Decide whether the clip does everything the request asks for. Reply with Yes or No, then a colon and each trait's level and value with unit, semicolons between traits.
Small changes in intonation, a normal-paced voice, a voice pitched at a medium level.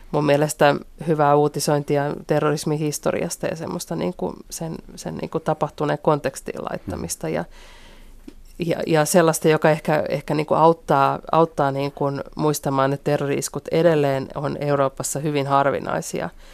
Yes: narrow, 2.2 semitones; average, 135 wpm; medium, 150 Hz